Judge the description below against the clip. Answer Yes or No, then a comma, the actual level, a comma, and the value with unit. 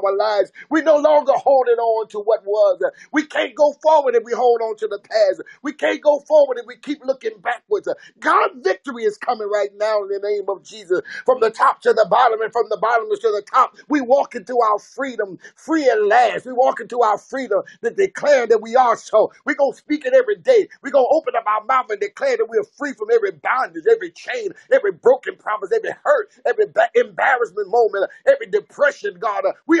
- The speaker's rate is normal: No, fast, 215 wpm